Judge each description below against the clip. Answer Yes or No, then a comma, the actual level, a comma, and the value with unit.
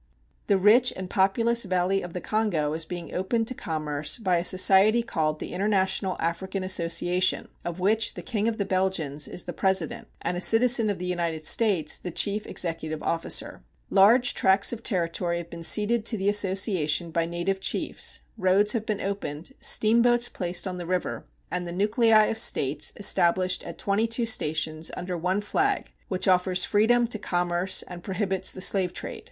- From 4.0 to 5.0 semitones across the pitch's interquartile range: No, average, 3.5 semitones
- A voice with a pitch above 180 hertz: Yes, high, 190 Hz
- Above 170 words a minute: Yes, average, 180 wpm